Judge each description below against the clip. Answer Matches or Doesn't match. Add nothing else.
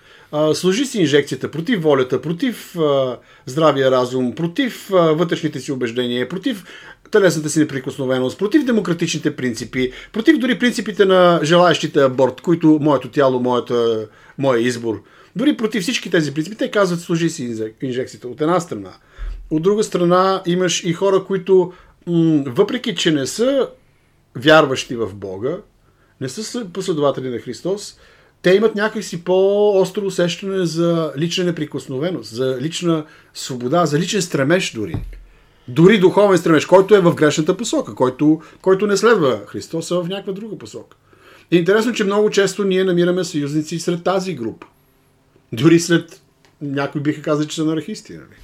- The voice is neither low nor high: Matches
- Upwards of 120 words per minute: Matches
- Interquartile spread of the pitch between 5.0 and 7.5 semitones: Matches